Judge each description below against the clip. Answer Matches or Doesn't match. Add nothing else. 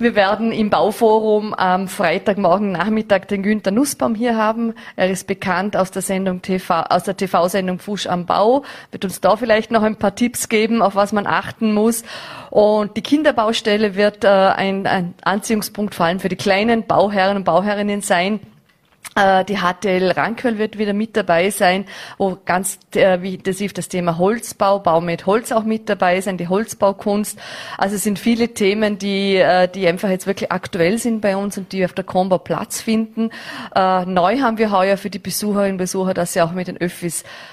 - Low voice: Doesn't match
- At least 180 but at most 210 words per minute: Matches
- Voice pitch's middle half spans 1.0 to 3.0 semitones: Matches